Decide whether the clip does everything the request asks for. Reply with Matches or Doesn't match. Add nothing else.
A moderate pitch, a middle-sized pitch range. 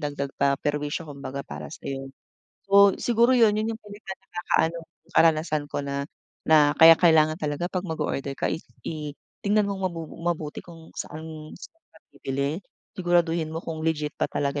Matches